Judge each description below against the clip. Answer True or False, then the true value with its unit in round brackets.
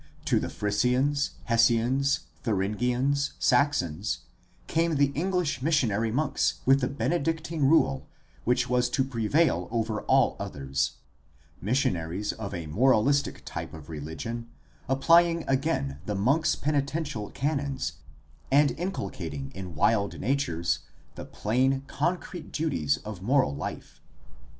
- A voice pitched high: False (125 Hz)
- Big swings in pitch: True (5.8 semitones)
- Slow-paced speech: True (115 wpm)